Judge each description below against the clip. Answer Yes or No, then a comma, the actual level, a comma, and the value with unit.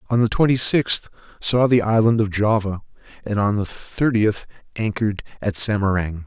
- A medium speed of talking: Yes, average, 155 wpm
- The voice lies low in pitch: Yes, low, 110 Hz